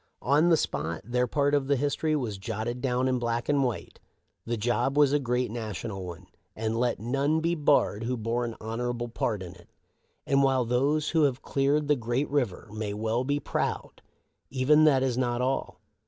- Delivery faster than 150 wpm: Yes, average, 200 wpm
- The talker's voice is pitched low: Yes, low, 125 Hz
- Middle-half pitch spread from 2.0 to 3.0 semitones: No, average, 3.7 semitones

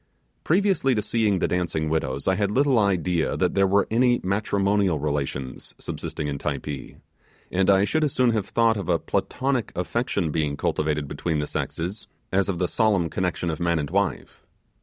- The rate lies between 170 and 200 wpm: Yes, average, 180 wpm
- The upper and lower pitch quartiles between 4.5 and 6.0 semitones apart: Yes, wide, 5.6 semitones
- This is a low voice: Yes, very low, 95 Hz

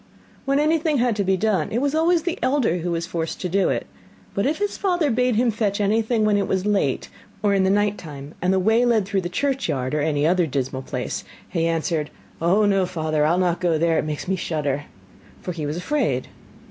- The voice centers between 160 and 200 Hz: Yes, high, 190 Hz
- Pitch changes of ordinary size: No, wide, 5.9 semitones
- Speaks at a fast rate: Yes, fast, 225 wpm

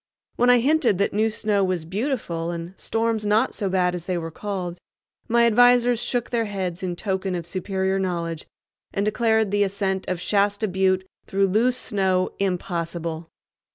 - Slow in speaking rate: No, average, 165 wpm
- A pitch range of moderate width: Yes, average, 3.6 semitones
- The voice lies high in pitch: Yes, high, 195 Hz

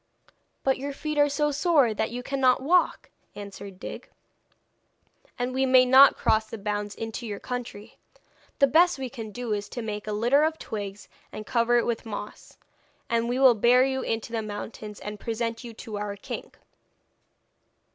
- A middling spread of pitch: Yes, average, 3.8 semitones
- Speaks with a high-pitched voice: Yes, high, 235 Hz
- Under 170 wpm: No, average, 175 wpm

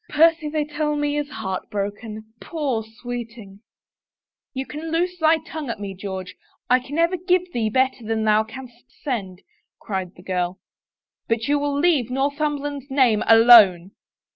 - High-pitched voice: Yes, very high, 250 Hz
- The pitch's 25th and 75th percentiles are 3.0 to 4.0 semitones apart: No, wide, 5.6 semitones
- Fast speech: No, average, 175 wpm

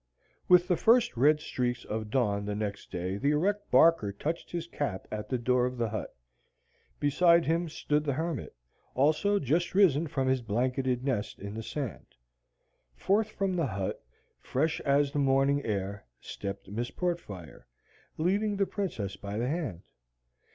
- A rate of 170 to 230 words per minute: No, average, 160 wpm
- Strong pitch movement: Yes, wide, 7.6 semitones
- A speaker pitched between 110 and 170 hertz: Yes, low, 135 Hz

